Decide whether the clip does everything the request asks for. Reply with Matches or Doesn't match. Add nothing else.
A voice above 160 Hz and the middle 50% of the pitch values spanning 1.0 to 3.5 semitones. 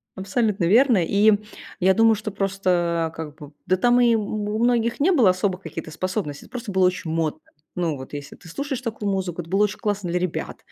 Doesn't match